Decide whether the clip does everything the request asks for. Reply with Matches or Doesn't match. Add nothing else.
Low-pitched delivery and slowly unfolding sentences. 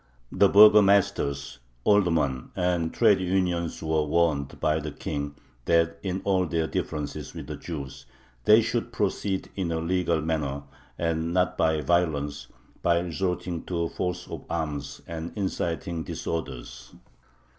Matches